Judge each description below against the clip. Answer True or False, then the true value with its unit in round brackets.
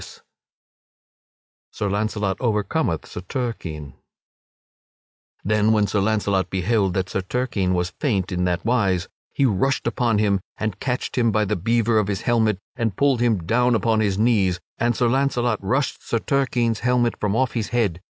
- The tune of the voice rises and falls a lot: False (3.7 semitones)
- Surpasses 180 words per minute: False (165 wpm)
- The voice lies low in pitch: True (110 Hz)